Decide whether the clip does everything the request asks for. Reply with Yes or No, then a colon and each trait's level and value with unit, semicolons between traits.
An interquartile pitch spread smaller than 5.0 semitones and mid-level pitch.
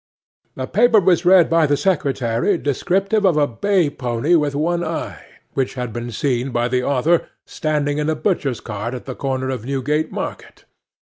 No: average, 5.3 semitones; medium, 145 Hz